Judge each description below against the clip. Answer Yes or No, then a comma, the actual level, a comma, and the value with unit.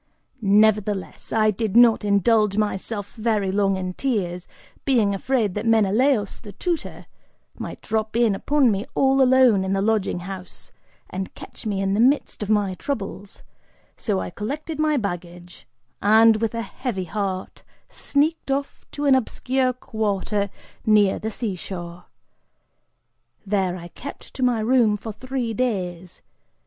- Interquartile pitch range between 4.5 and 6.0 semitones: No, average, 3.9 semitones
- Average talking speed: Yes, average, 145 wpm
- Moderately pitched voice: No, high, 215 Hz